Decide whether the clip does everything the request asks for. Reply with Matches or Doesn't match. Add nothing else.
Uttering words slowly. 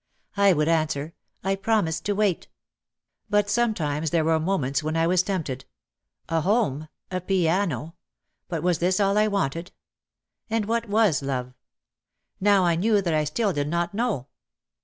Doesn't match